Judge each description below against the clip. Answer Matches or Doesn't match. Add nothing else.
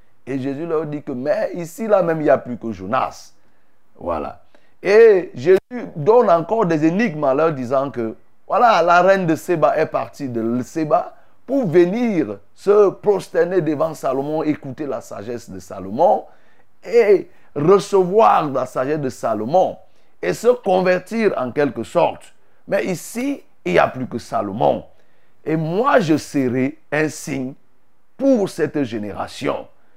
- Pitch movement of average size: Doesn't match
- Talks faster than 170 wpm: Doesn't match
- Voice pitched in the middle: Matches